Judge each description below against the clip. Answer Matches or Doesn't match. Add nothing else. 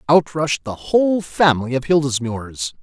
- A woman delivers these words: Doesn't match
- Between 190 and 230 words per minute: Doesn't match